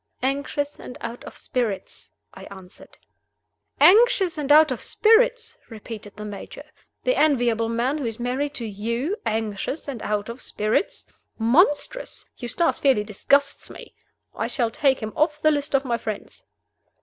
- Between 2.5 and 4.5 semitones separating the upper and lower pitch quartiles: No, average, 5.1 semitones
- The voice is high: Yes, very high, 255 Hz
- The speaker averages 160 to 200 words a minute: No, average, 150 wpm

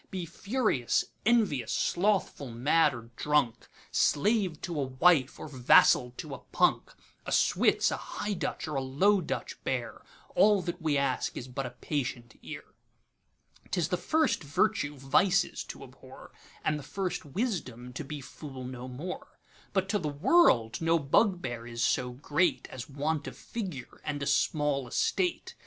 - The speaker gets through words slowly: No, average, 145 wpm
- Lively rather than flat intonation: Yes, wide, 6.1 semitones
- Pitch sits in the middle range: Yes, medium, 150 Hz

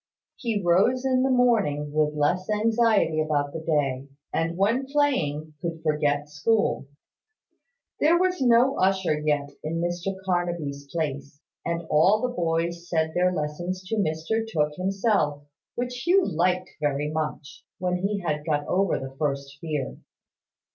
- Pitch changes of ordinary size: No, wide, 5.8 semitones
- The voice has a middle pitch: Yes, medium, 170 Hz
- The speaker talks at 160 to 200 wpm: No, average, 145 wpm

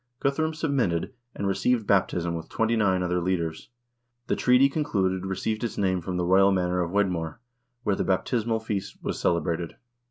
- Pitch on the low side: Yes, very low, 95 Hz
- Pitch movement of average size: Yes, average, 4.0 semitones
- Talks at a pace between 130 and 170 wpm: Yes, average, 165 wpm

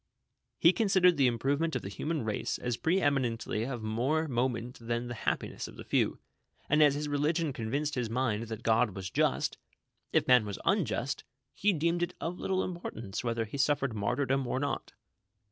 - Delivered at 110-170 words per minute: No, average, 180 wpm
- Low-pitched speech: Yes, low, 130 Hz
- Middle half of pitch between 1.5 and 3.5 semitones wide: No, average, 5.1 semitones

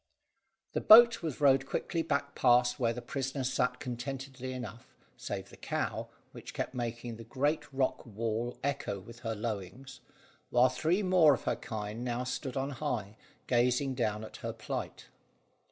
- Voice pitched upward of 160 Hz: No, low, 125 Hz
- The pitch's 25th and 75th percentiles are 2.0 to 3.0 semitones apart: Yes, average, 2.7 semitones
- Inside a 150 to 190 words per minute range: Yes, average, 160 wpm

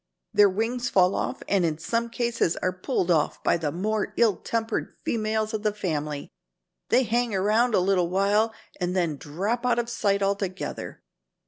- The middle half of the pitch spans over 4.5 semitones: No, average, 4.0 semitones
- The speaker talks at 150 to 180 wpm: Yes, average, 175 wpm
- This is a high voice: Yes, high, 200 Hz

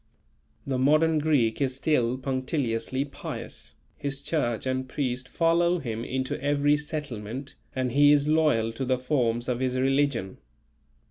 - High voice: No, low, 130 Hz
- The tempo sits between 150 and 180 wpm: No, average, 140 wpm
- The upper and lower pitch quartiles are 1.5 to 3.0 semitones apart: Yes, average, 2.7 semitones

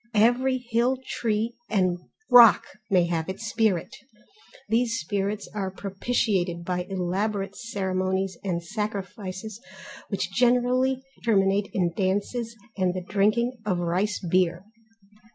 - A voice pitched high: Yes, high, 200 Hz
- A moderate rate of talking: No, slow, 115 wpm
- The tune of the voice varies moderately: Yes, average, 3.7 semitones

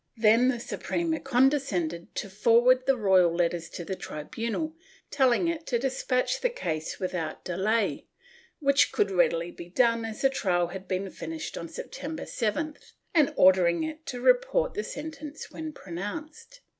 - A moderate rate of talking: Yes, average, 155 wpm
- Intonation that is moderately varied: No, wide, 8.5 semitones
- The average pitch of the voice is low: No, high, 235 Hz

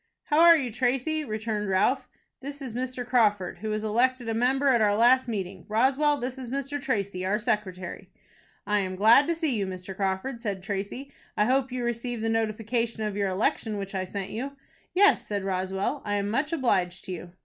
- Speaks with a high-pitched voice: Yes, high, 225 Hz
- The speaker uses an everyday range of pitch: Yes, average, 4.5 semitones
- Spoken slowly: No, average, 200 wpm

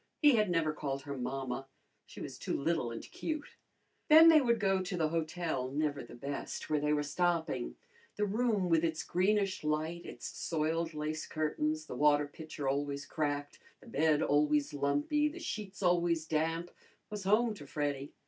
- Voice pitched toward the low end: No, medium, 155 Hz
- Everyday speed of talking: Yes, average, 175 wpm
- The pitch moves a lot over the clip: No, average, 4.2 semitones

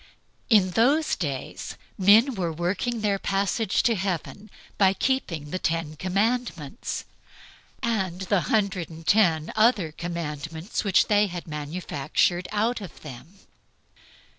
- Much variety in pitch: No, average, 4.5 semitones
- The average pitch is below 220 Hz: Yes, medium, 185 Hz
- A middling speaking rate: No, slow, 120 wpm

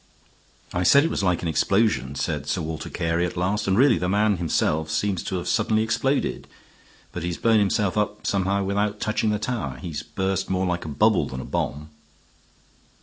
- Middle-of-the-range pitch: No, very low, 95 Hz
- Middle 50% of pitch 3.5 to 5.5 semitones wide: Yes, average, 4.0 semitones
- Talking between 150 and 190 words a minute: No, average, 200 wpm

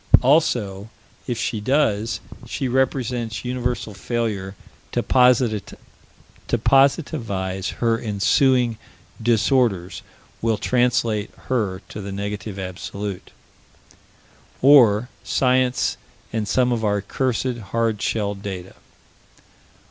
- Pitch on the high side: No, low, 115 Hz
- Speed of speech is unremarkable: No, slow, 90 wpm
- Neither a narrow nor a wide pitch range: Yes, average, 3.5 semitones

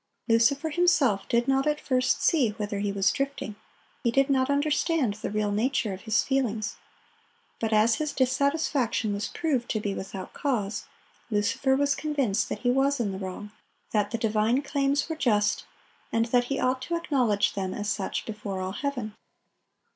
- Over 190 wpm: No, average, 175 wpm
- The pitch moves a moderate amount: Yes, average, 4.9 semitones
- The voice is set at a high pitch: Yes, high, 240 Hz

